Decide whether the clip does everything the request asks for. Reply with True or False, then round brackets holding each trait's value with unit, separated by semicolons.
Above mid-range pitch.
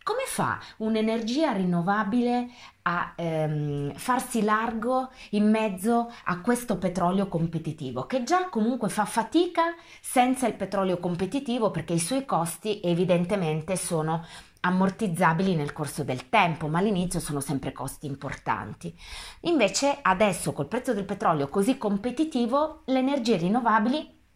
True (205 Hz)